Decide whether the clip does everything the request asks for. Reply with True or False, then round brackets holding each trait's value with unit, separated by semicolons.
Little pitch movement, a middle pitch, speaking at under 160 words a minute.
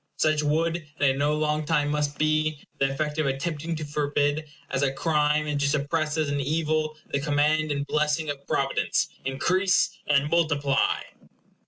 False (1.4 semitones; 150 Hz; 170 wpm)